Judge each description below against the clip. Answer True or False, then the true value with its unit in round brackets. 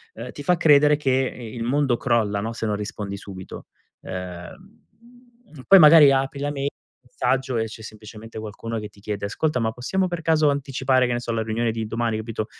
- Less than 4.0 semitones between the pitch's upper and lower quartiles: False (4.5 semitones)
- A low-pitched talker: True (120 Hz)